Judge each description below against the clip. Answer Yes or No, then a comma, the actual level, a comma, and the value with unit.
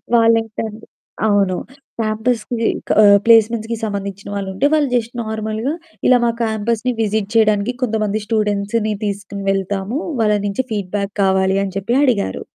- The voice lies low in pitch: No, high, 215 Hz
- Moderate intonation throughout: No, narrow, 2.2 semitones